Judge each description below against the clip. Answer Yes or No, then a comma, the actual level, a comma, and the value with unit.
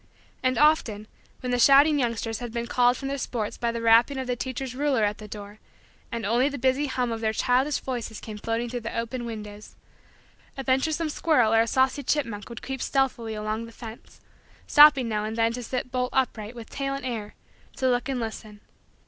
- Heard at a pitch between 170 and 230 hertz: No, high, 240 Hz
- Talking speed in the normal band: No, fast, 210 wpm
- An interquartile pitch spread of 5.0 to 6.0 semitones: No, average, 2.9 semitones